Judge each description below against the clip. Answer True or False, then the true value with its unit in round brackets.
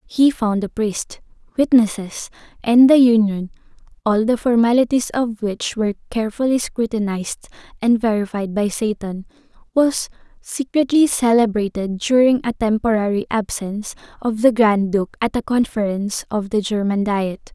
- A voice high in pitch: True (220 Hz)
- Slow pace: True (125 wpm)